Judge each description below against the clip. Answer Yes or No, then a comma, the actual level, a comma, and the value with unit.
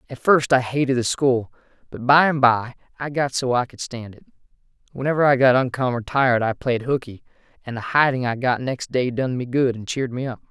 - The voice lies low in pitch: Yes, low, 125 Hz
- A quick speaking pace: Yes, fast, 225 wpm